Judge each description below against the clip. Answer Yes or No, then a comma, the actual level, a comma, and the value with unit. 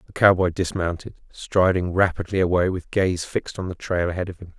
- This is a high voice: No, very low, 90 Hz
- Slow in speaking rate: No, average, 195 wpm